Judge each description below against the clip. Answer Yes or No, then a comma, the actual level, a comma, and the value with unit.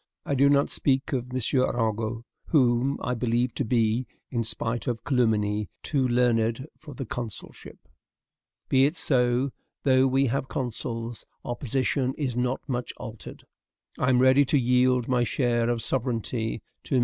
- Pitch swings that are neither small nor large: No, narrow, 2.1 semitones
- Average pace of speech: Yes, average, 160 wpm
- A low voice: Yes, low, 125 Hz